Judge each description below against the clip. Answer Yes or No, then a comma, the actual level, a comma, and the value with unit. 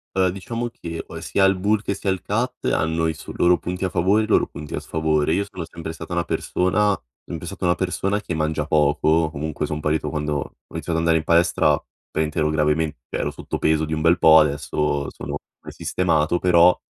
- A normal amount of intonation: Yes, average, 3.0 semitones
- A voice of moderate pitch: No, very low, 80 Hz